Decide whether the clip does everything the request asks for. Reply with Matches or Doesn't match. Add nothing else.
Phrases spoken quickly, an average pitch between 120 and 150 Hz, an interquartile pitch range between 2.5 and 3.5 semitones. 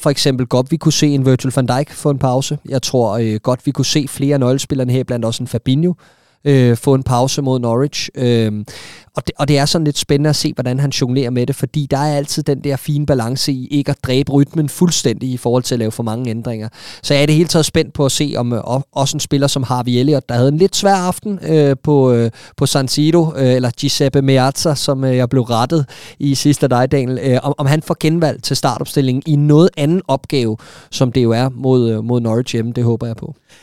Matches